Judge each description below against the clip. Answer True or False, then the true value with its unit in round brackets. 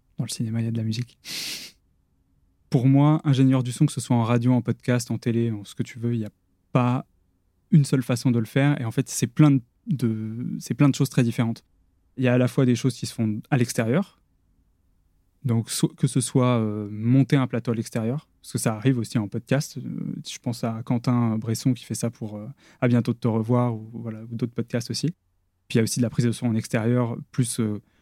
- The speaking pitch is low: True (120 Hz)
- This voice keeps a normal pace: False (250 wpm)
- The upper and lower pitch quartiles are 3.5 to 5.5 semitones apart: False (3.0 semitones)